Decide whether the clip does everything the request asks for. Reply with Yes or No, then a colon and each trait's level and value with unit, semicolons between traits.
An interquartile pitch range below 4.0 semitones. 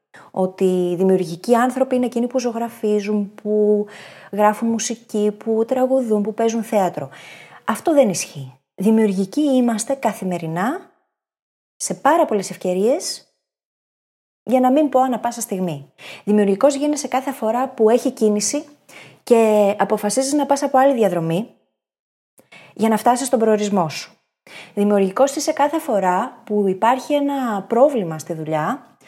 No: average, 4.7 semitones